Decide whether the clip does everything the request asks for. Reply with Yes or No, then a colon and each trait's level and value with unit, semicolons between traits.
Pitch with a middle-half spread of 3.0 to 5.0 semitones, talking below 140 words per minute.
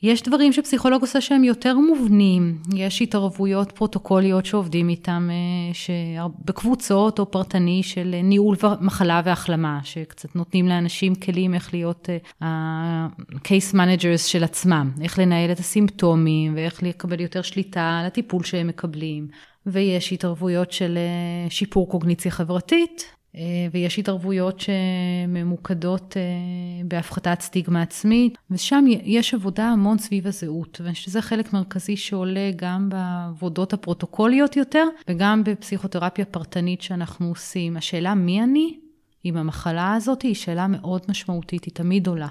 No: narrow, 2.5 semitones; average, 125 wpm